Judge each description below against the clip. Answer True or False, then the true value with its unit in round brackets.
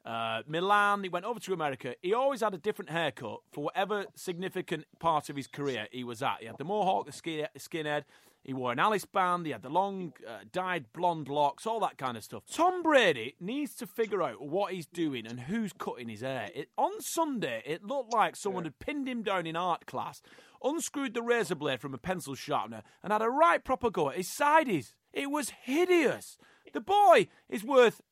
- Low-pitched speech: False (185 Hz)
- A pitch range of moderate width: False (8.4 semitones)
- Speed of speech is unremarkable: False (215 wpm)